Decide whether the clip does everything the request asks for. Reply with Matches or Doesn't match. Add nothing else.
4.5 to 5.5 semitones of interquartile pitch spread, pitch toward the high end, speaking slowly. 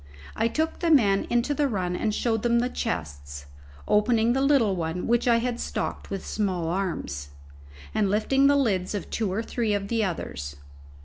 Doesn't match